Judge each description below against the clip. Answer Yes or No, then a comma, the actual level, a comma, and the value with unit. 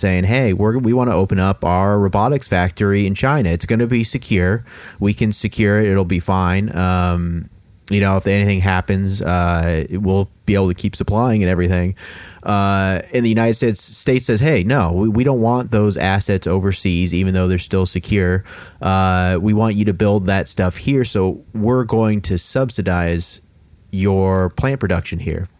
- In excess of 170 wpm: Yes, average, 185 wpm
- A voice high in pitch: No, very low, 95 Hz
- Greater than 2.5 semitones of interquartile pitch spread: Yes, average, 2.9 semitones